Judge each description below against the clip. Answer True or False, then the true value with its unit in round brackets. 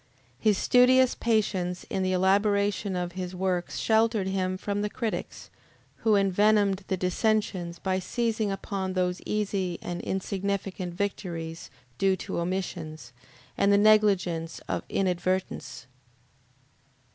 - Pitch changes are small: True (2.3 semitones)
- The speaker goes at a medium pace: False (120 wpm)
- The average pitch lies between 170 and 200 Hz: True (190 Hz)